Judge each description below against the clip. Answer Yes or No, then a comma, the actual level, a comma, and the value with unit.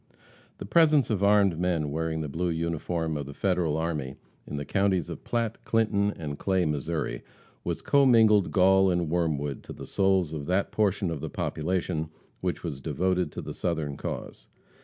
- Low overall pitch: Yes, very low, 85 Hz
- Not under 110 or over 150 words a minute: No, average, 180 wpm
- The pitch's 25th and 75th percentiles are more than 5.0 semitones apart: No, average, 4.0 semitones